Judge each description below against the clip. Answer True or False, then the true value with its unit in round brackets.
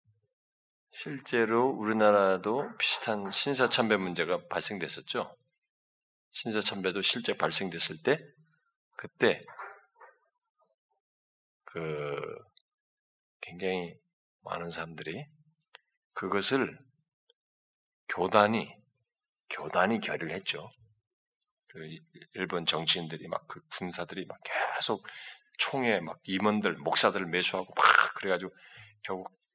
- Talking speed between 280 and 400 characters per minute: False (200 characters per minute)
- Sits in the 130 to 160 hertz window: True (135 Hz)